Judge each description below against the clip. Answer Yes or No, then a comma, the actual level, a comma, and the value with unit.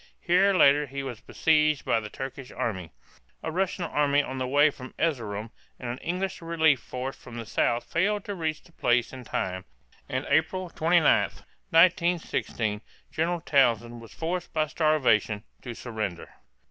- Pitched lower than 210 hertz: Yes, medium, 140 Hz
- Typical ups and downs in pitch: No, wide, 5.7 semitones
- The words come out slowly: No, average, 160 wpm